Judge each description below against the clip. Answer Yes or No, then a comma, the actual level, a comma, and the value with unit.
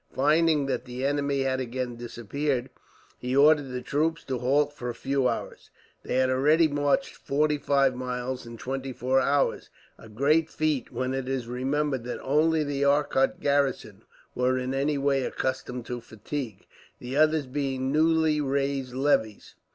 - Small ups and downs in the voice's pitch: Yes, narrow, 2.3 semitones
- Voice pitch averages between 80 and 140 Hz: Yes, low, 135 Hz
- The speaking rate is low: No, average, 160 wpm